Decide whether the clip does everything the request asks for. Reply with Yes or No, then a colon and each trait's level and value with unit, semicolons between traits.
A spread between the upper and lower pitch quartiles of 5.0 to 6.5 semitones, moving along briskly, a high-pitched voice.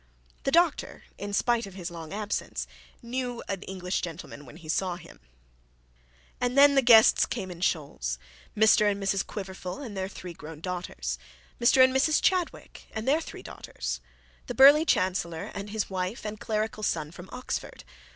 No: average, 5.3 semitones; average, 170 wpm; high, 200 Hz